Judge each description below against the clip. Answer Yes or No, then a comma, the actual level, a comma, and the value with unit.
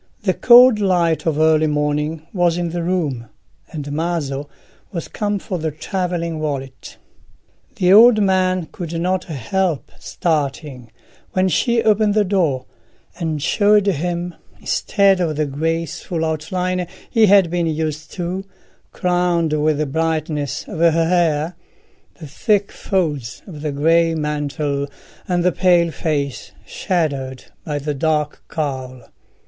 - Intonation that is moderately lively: Yes, average, 3.4 semitones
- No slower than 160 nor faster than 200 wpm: No, slow, 135 wpm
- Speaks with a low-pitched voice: No, medium, 165 Hz